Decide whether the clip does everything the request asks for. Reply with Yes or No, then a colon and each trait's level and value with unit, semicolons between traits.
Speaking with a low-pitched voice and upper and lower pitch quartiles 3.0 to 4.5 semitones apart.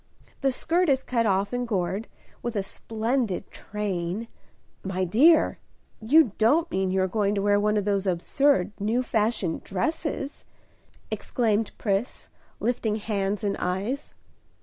No: high, 210 Hz; average, 4.0 semitones